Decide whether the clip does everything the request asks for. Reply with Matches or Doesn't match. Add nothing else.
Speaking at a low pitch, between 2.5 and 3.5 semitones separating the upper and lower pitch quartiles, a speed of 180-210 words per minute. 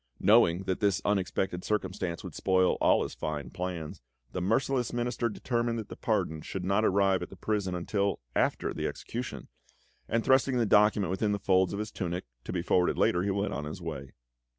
Matches